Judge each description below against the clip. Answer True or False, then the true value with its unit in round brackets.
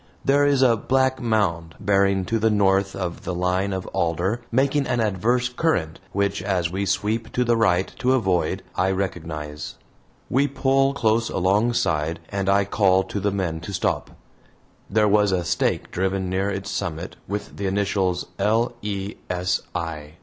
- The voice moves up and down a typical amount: True (3.7 semitones)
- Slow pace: False (165 wpm)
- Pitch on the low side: True (100 Hz)